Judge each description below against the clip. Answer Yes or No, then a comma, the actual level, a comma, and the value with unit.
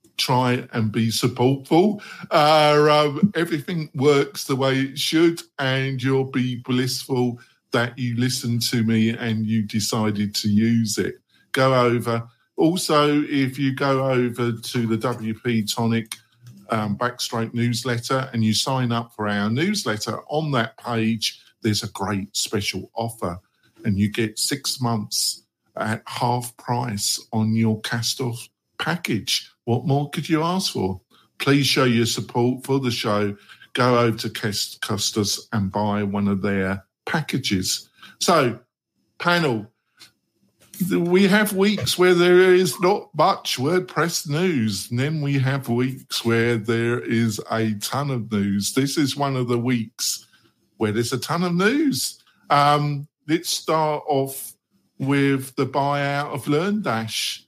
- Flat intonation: No, average, 4.1 semitones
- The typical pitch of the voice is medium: No, low, 125 Hz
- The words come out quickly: No, average, 145 wpm